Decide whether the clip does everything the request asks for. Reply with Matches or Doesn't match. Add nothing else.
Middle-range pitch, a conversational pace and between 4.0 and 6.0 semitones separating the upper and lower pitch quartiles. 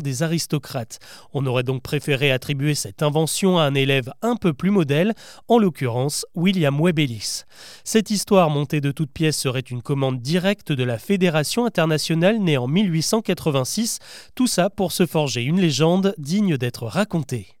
Matches